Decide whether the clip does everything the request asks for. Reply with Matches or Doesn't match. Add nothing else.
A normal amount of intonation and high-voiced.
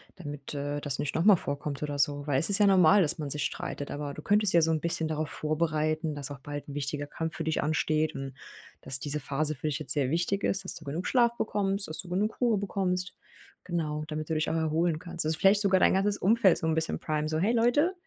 Doesn't match